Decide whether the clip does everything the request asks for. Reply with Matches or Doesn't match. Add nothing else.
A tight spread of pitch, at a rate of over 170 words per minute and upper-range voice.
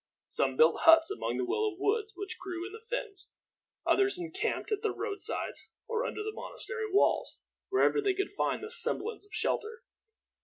Matches